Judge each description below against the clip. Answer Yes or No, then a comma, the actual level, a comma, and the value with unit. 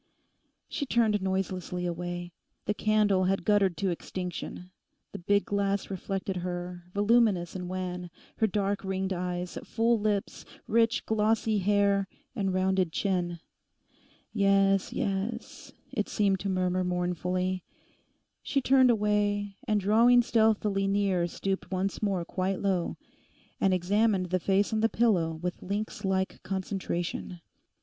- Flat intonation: Yes, narrow, 2.3 semitones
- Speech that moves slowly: Yes, slow, 130 wpm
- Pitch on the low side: No, high, 195 Hz